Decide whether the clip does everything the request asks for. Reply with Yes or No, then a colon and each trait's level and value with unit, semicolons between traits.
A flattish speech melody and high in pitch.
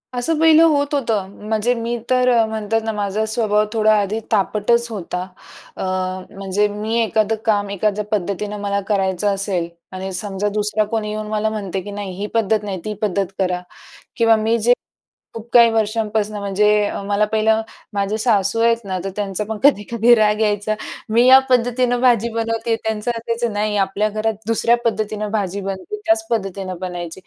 Yes: narrow, 2.1 semitones; high, 215 Hz